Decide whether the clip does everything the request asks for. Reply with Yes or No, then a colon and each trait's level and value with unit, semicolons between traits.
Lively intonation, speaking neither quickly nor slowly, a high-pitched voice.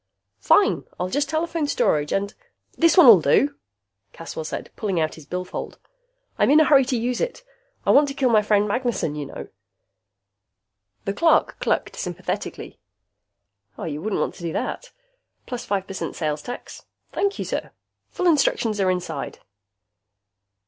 Yes: wide, 8.1 semitones; average, 155 wpm; high, 215 Hz